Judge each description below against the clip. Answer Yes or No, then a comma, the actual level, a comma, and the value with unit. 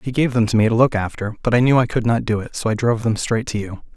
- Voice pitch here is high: No, low, 115 Hz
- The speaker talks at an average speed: No, fast, 350 wpm